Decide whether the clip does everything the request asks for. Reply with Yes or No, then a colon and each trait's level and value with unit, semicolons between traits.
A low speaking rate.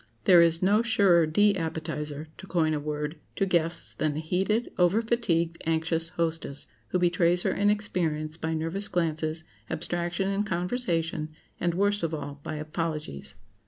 No: average, 145 wpm